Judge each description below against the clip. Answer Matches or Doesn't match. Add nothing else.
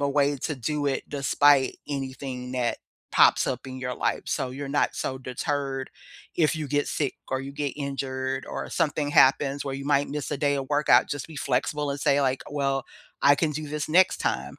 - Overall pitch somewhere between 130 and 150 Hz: Matches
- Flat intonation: Matches